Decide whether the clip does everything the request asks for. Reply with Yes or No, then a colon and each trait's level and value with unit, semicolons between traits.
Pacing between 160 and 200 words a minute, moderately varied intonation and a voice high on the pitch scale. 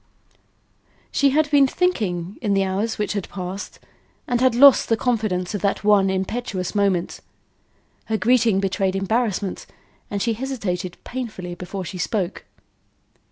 No: average, 140 wpm; average, 4.1 semitones; high, 205 Hz